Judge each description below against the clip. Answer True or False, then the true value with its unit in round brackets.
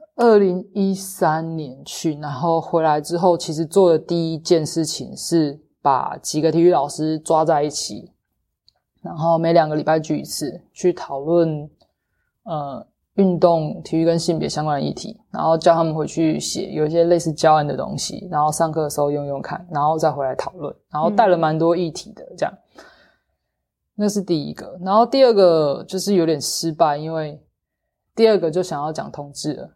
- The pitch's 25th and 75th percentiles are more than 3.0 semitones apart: False (2.7 semitones)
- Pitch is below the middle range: False (165 Hz)